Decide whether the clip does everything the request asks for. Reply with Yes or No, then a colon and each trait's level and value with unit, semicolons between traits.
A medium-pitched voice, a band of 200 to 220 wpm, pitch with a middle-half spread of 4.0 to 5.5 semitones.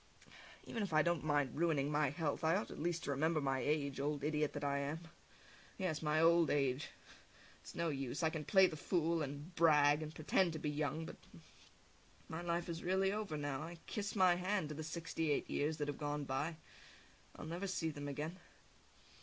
No: medium, 155 Hz; fast, 205 wpm; narrow, 2.6 semitones